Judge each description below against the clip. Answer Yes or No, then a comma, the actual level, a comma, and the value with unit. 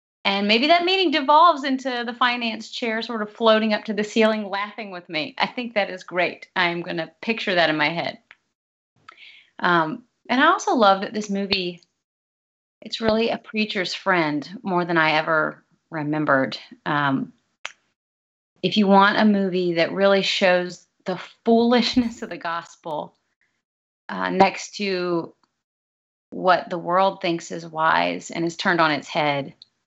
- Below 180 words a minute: Yes, average, 160 wpm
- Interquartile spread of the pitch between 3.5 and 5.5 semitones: Yes, average, 5.0 semitones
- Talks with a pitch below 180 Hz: No, high, 195 Hz